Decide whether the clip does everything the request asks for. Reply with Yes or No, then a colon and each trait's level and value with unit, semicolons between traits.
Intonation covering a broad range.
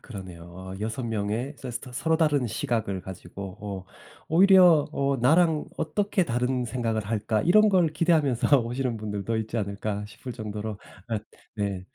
Yes: wide, 5.8 semitones